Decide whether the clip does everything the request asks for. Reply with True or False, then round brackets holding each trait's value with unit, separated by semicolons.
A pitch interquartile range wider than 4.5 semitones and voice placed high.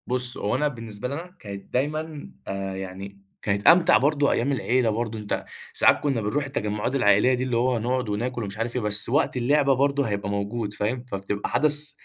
False (5.0 semitones; 120 Hz)